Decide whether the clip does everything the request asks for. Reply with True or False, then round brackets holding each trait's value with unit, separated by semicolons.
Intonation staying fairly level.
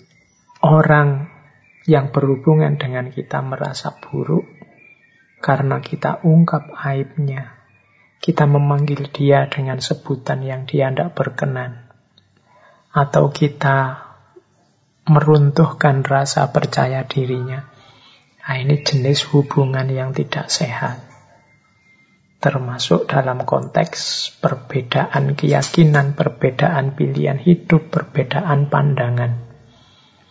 True (2.3 semitones)